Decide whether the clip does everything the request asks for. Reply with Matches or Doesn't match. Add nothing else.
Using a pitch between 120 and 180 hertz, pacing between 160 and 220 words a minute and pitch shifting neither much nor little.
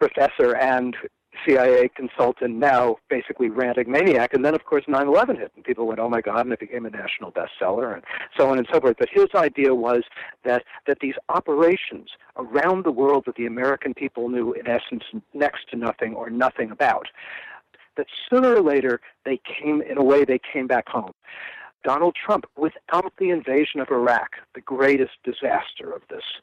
Doesn't match